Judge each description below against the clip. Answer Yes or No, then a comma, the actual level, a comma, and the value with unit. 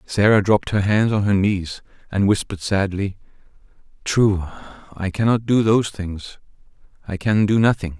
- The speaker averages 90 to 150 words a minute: Yes, average, 145 wpm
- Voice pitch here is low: Yes, low, 100 Hz